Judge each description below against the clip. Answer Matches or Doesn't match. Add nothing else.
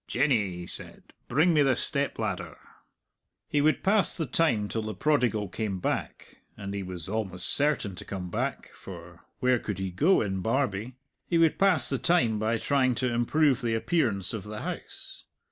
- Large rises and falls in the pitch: Matches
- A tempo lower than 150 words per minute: Doesn't match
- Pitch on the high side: Doesn't match